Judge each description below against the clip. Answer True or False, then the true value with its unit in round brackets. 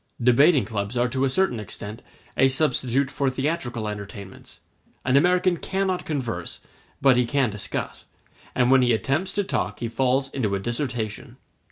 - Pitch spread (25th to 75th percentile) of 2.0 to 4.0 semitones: True (3.3 semitones)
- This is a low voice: True (130 Hz)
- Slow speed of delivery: False (160 wpm)